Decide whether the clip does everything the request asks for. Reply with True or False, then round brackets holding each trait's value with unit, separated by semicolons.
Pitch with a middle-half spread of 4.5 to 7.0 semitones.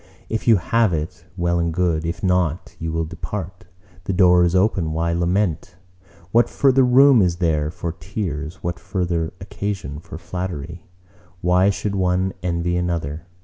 False (2.4 semitones)